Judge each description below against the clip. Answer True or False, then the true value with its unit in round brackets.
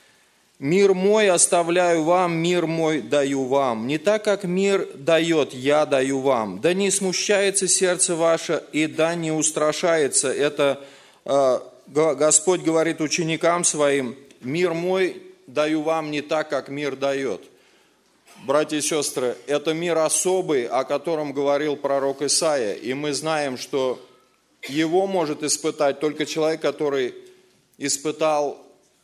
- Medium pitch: True (155 Hz)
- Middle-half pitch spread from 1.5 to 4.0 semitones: True (3.5 semitones)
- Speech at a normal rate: True (130 wpm)